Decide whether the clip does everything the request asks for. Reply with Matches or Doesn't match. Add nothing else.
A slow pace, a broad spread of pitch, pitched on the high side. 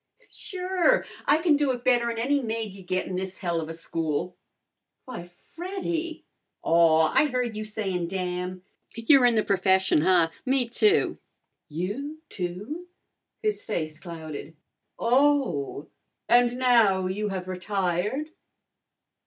Matches